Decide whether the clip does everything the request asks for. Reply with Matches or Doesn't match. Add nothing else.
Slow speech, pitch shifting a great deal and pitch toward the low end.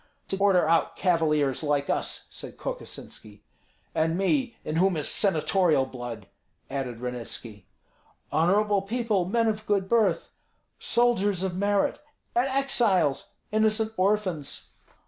Doesn't match